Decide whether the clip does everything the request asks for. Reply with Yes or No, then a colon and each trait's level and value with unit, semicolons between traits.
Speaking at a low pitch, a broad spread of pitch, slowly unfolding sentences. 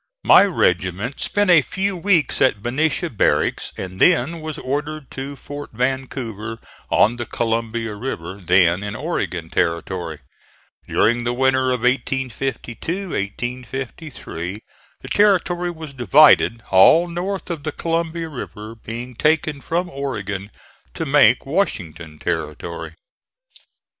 Yes: low, 130 Hz; wide, 6.8 semitones; slow, 120 wpm